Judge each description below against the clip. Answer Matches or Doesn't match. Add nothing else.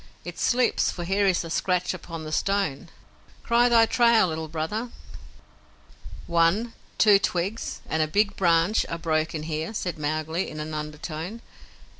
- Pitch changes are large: Doesn't match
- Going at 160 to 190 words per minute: Doesn't match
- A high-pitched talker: Doesn't match